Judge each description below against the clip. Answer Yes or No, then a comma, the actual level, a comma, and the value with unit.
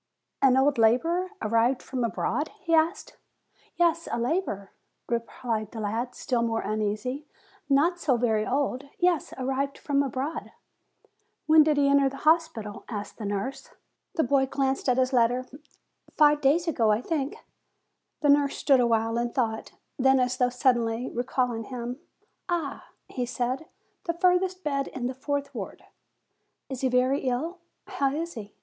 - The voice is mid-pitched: No, very high, 265 Hz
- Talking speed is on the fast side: No, average, 155 wpm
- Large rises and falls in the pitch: No, average, 3.7 semitones